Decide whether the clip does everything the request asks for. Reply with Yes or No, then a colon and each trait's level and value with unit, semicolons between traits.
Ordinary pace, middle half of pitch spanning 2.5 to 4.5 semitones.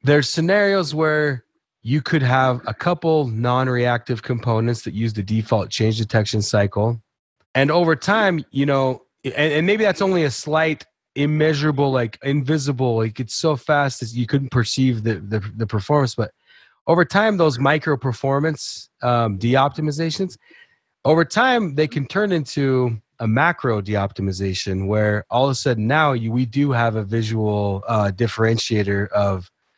No: average, 155 wpm; wide, 5.5 semitones